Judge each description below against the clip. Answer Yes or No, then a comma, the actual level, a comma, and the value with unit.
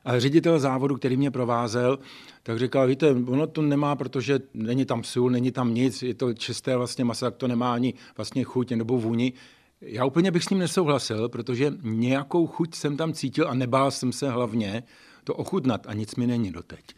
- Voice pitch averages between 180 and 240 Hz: No, low, 125 Hz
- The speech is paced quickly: Yes, fast, 200 wpm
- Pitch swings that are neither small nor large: No, narrow, 2.3 semitones